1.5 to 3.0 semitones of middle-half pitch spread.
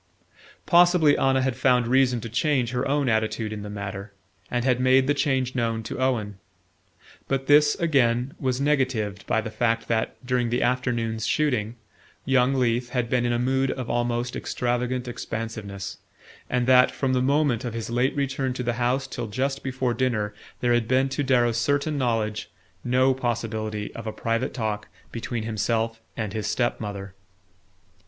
Yes: narrow, 2.6 semitones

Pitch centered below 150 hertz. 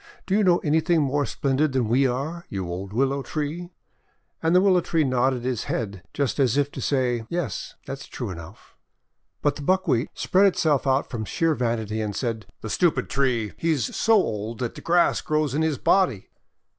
Yes: low, 135 Hz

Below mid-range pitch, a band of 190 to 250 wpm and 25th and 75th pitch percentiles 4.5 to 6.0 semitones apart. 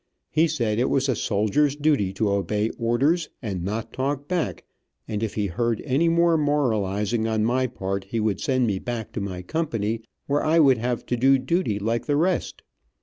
Yes: low, 120 Hz; average, 195 wpm; wide, 5.4 semitones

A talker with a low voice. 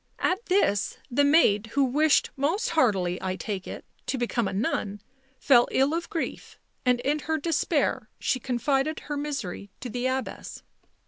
No: very high, 265 Hz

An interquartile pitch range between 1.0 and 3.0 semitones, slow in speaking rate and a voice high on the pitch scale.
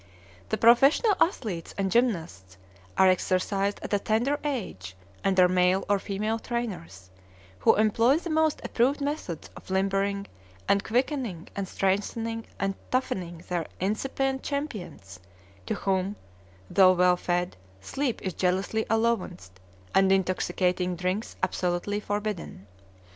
No: average, 4.3 semitones; slow, 120 wpm; high, 195 Hz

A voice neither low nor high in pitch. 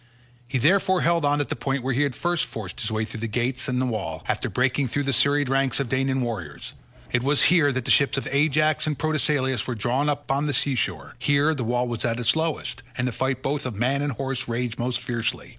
No: low, 130 Hz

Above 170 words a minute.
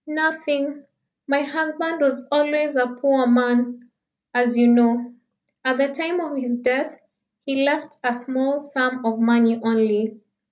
No: average, 145 wpm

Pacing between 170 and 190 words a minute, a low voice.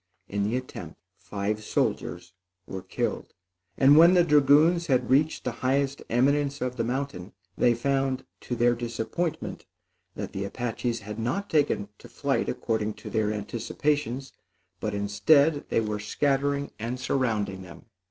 No: average, 145 wpm; low, 125 Hz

